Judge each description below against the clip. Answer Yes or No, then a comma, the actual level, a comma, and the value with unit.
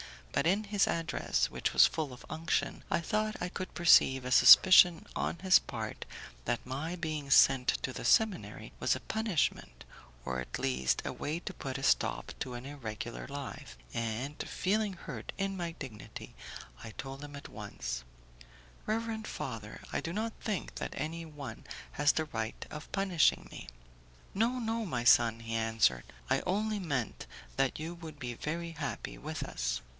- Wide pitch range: Yes, wide, 7.4 semitones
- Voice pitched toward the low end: No, medium, 150 Hz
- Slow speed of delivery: No, average, 170 wpm